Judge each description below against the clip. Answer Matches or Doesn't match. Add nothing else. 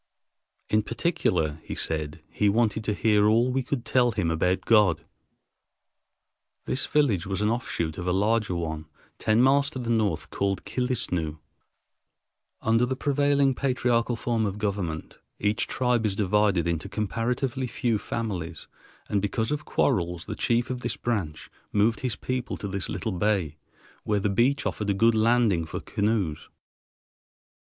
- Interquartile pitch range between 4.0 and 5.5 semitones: Matches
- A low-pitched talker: Matches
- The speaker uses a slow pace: Doesn't match